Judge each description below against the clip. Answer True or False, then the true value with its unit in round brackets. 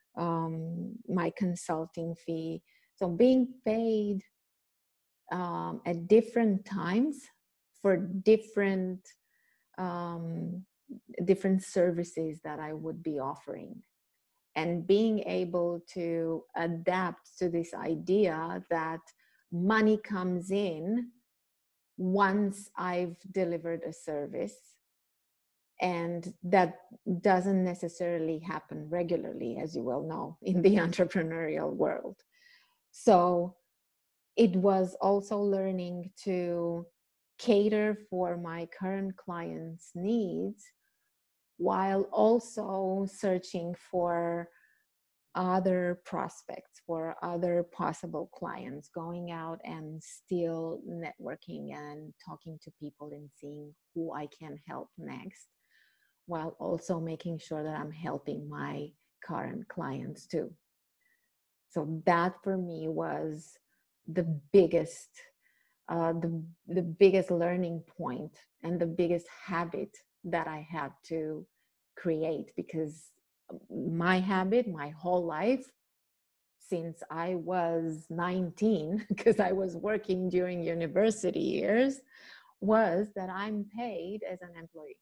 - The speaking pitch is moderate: True (180 Hz)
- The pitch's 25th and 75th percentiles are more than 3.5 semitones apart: False (3.0 semitones)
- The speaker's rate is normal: False (105 wpm)